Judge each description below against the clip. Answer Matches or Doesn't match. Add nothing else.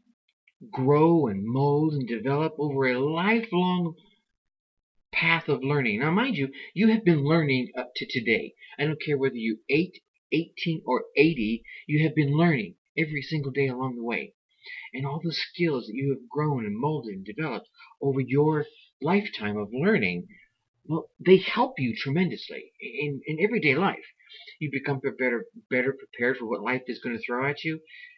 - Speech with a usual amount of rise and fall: Matches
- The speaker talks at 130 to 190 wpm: Matches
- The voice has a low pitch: Doesn't match